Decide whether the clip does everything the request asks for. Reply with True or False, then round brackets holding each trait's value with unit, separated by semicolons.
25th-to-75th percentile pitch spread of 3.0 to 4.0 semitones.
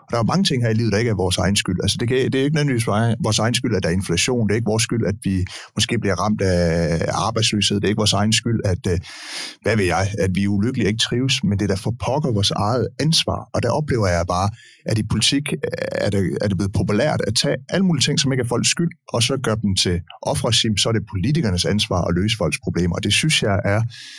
True (3.7 semitones)